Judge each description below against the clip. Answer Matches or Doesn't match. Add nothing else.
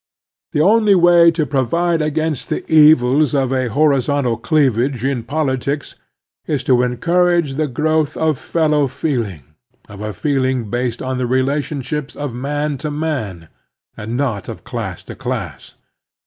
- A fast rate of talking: Doesn't match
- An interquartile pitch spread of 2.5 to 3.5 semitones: Doesn't match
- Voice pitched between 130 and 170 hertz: Matches